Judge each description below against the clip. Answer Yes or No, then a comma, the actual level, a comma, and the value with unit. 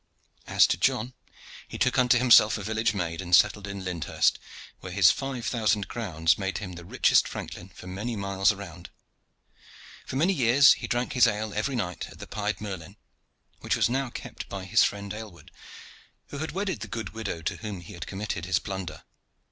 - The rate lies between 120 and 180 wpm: No, average, 190 wpm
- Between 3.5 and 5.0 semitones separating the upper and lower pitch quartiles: Yes, average, 4.0 semitones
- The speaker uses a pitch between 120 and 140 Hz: No, low, 105 Hz